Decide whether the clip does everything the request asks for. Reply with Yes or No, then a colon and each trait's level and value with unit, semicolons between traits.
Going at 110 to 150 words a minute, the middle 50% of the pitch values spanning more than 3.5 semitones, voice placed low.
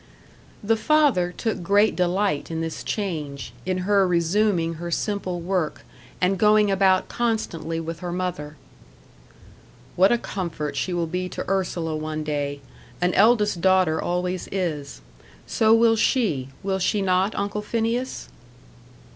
No: average, 140 wpm; average, 3.9 semitones; medium, 185 Hz